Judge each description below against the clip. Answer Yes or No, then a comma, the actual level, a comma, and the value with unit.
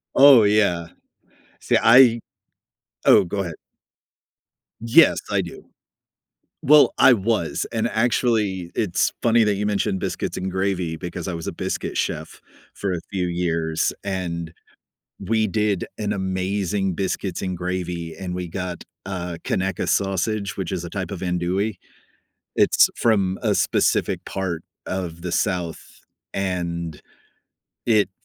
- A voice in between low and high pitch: No, very low, 95 Hz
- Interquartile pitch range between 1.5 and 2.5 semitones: No, average, 2.9 semitones